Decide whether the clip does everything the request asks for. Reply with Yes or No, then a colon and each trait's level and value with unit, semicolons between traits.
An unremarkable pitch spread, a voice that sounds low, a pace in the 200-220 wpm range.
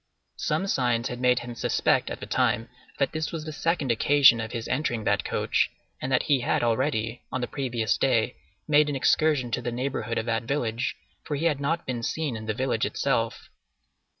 Yes: average, 3.8 semitones; low, 125 Hz; fast, 205 wpm